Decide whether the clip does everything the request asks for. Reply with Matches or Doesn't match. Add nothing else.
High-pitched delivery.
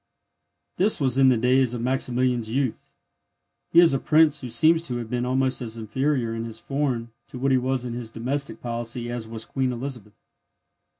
Doesn't match